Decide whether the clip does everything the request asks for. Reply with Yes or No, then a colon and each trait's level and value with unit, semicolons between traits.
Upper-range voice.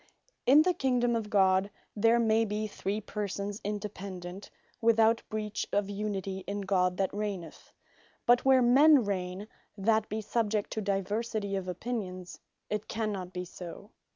Yes: high, 205 Hz